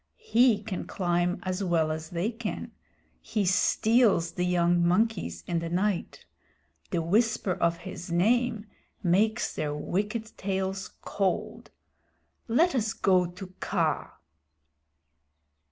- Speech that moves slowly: Yes, slow, 120 wpm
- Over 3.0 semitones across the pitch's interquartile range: Yes, average, 4.0 semitones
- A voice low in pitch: No, medium, 185 Hz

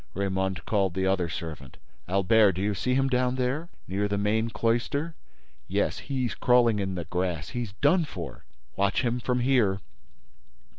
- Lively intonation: No, average, 4.7 semitones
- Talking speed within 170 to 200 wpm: No, average, 160 wpm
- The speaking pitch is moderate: No, low, 105 Hz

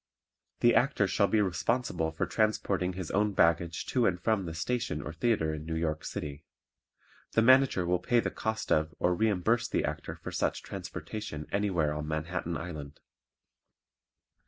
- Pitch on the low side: Yes, very low, 90 Hz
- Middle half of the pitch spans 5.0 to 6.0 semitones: Yes, wide, 5.4 semitones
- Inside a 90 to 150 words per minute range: No, average, 160 wpm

